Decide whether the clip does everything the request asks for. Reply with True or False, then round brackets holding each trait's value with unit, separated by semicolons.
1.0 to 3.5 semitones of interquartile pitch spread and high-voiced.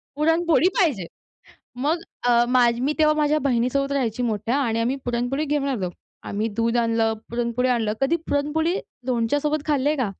False (4.0 semitones; 255 Hz)